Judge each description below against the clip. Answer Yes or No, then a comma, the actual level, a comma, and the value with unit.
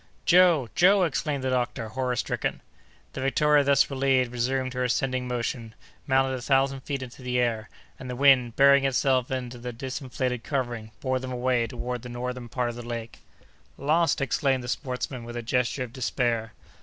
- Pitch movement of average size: No, narrow, 1.9 semitones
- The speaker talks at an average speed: Yes, average, 180 wpm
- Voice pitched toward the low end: Yes, low, 130 Hz